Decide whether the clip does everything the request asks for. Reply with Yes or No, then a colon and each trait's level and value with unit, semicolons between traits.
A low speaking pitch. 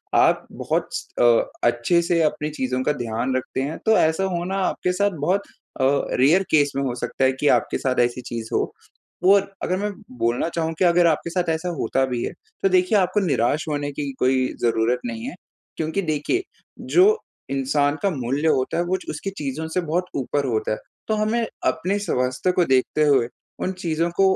No: medium, 155 Hz